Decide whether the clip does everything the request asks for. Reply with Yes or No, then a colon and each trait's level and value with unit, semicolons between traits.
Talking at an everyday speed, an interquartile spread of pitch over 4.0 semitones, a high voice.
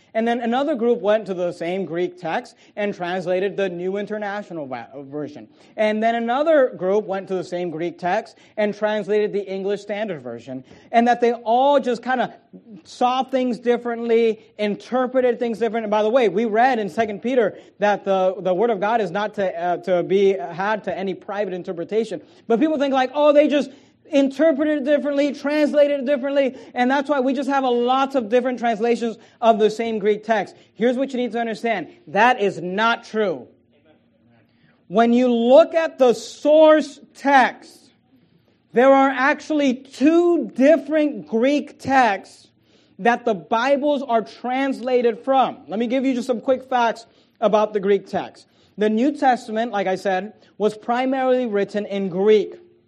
Yes: average, 175 wpm; average, 4.4 semitones; high, 230 Hz